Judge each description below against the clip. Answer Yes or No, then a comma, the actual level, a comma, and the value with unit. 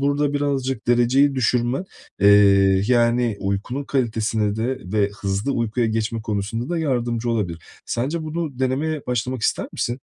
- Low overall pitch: Yes, low, 120 Hz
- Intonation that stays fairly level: No, average, 3.5 semitones